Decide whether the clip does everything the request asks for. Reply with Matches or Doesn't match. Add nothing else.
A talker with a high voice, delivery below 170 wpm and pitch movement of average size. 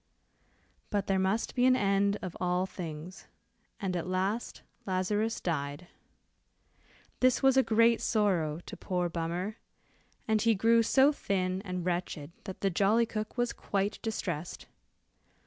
Matches